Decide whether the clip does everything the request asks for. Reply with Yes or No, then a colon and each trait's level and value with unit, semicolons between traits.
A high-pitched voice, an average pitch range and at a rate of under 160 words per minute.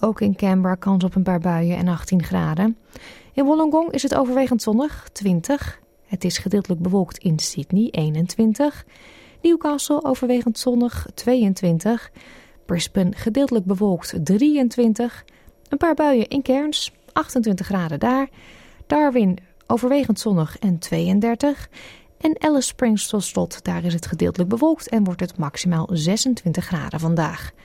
No: high, 210 Hz; wide, 6.4 semitones; slow, 135 wpm